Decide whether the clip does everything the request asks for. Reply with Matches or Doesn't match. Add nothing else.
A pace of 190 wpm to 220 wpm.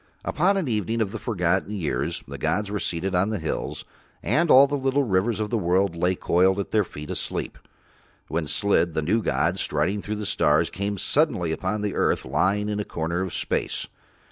Matches